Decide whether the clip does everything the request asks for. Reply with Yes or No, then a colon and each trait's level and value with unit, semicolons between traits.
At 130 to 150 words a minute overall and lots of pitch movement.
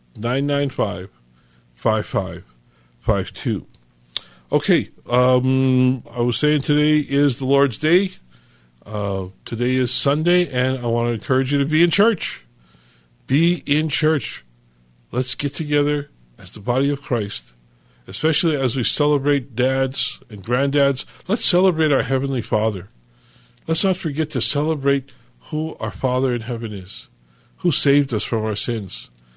Yes: average, 145 wpm; wide, 6.8 semitones